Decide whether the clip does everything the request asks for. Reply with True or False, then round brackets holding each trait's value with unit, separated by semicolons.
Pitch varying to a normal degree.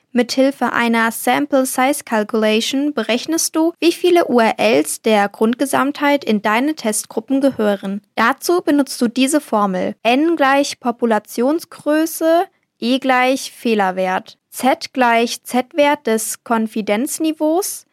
True (4.6 semitones)